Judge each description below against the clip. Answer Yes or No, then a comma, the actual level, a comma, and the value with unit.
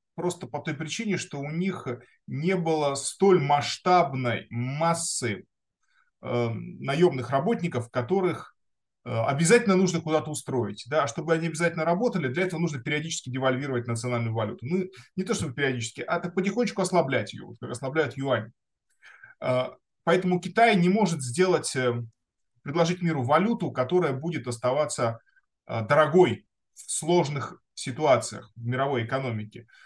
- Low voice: No, medium, 155 Hz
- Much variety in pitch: Yes, wide, 6.0 semitones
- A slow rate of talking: No, average, 135 wpm